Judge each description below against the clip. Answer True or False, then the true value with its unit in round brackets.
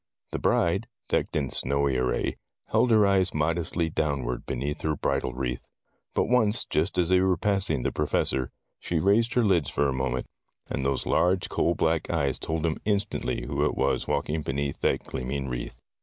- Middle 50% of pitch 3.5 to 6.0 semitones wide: True (5.6 semitones)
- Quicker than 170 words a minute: True (180 wpm)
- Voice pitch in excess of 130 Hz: False (80 Hz)